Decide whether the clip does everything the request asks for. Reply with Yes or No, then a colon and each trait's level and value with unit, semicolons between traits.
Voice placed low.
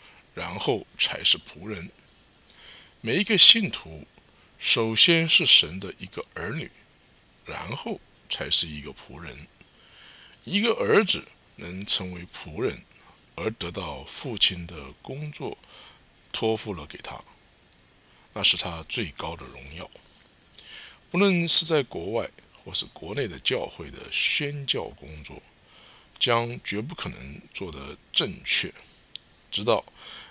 Yes: low, 100 Hz